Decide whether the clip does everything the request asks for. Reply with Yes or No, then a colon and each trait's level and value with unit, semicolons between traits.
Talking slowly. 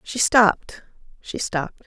Yes: slow, 130 wpm